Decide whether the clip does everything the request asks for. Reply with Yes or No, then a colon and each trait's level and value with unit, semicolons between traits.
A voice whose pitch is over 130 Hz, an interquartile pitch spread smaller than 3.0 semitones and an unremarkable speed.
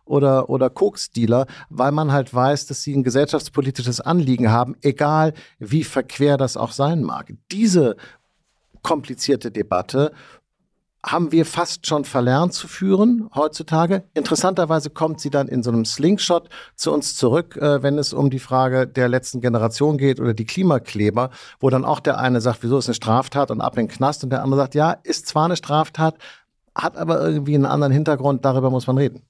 No: medium, 140 Hz; average, 3.3 semitones; average, 180 wpm